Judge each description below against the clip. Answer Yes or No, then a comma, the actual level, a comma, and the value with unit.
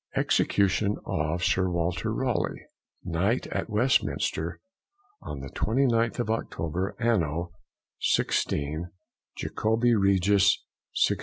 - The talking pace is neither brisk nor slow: No, slow, 95 wpm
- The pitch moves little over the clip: No, average, 4.9 semitones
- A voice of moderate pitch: No, very low, 95 Hz